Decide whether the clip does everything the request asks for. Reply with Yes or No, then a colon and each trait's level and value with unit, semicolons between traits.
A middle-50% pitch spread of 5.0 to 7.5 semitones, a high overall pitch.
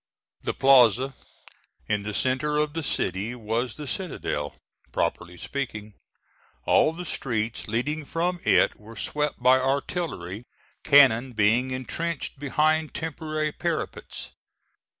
No: average, 5.3 semitones; low, 130 Hz